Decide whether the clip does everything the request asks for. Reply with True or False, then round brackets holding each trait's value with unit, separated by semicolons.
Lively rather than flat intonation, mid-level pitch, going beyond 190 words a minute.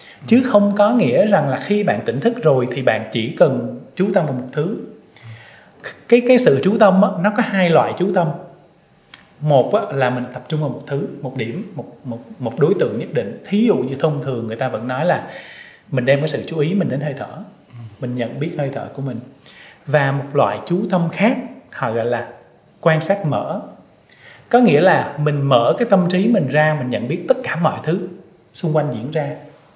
True (6.4 semitones; 155 Hz; 220 wpm)